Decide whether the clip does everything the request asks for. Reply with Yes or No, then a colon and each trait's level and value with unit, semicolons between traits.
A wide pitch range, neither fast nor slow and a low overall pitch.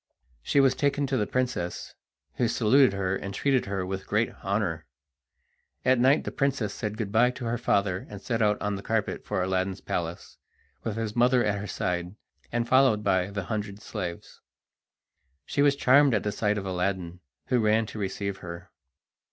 No: average, 4.3 semitones; average, 185 wpm; low, 105 Hz